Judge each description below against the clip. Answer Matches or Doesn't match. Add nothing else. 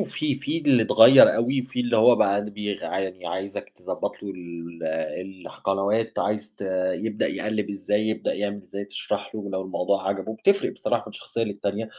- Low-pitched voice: Matches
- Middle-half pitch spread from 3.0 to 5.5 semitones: Doesn't match